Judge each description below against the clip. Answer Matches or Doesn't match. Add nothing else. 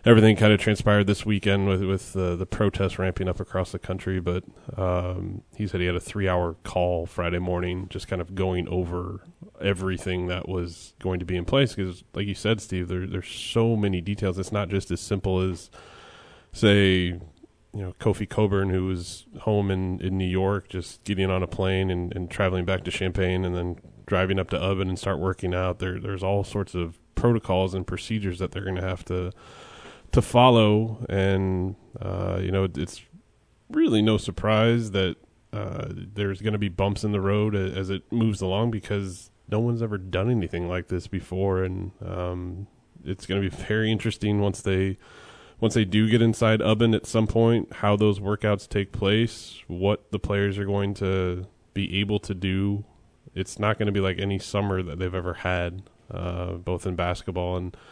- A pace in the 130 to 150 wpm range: Doesn't match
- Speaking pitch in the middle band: Doesn't match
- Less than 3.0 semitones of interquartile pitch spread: Matches